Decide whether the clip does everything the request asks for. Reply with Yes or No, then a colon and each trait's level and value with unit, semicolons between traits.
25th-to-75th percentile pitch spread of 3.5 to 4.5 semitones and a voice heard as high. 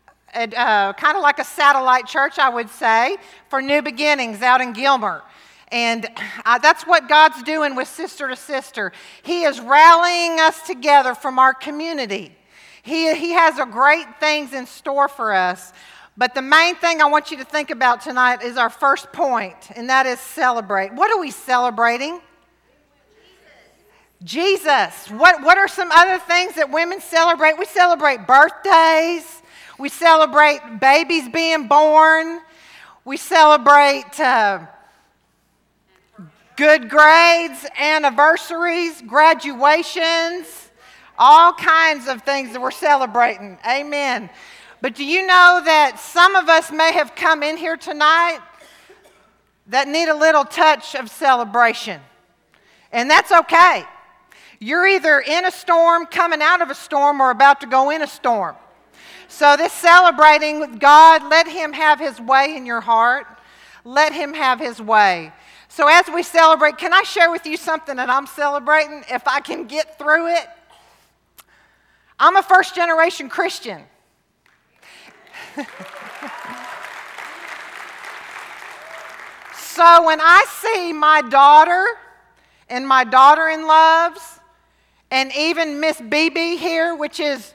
Yes: average, 3.9 semitones; very high, 300 Hz